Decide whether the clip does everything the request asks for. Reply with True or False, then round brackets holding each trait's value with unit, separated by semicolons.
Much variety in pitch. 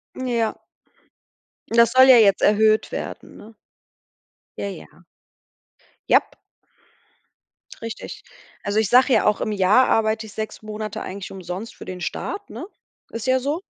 False (2.6 semitones)